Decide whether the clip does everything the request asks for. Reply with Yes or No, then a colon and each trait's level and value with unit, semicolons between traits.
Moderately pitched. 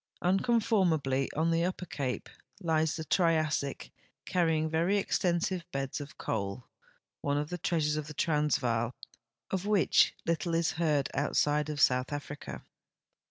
Yes: medium, 155 Hz